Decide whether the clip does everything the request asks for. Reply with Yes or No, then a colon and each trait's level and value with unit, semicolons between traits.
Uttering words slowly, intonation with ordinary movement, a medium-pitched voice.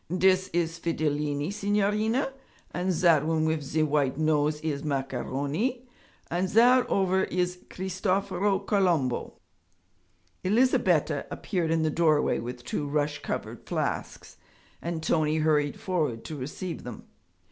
Yes: slow, 125 wpm; average, 4.2 semitones; medium, 165 Hz